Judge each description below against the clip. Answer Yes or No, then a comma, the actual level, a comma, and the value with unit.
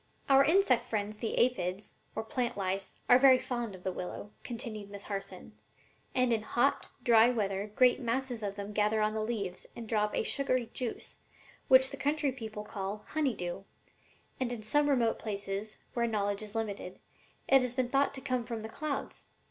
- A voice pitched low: No, high, 225 Hz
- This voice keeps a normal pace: Yes, average, 185 wpm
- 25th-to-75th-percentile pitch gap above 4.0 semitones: No, average, 3.6 semitones